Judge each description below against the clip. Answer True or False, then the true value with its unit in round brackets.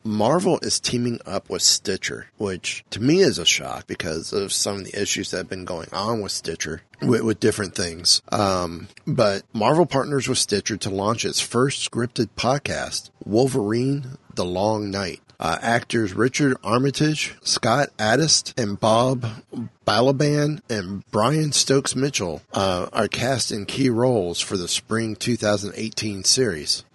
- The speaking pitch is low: True (115 Hz)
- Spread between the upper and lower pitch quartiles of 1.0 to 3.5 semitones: False (4.3 semitones)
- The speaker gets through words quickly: False (150 wpm)